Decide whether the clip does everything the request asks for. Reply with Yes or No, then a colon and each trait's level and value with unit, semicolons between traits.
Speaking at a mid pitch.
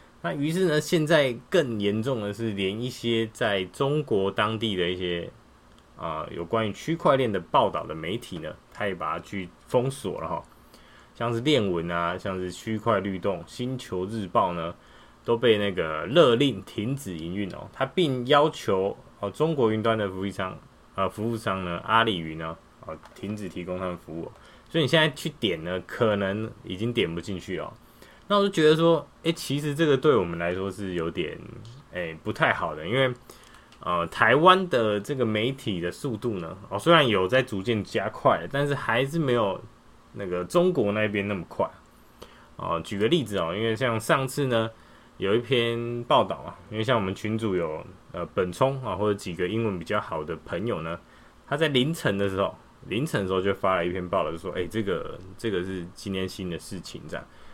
No: low, 110 Hz